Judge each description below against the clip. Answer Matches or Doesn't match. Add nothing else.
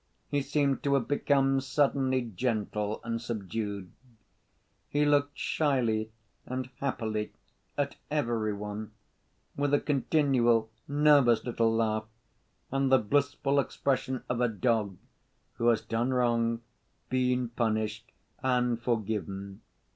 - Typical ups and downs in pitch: Matches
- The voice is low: Matches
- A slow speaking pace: Matches